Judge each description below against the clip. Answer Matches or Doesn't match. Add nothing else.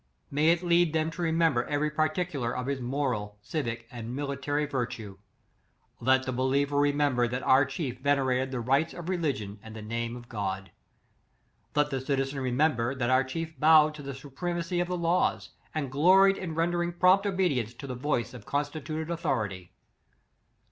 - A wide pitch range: Doesn't match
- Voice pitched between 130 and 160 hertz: Matches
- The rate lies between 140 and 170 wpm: Doesn't match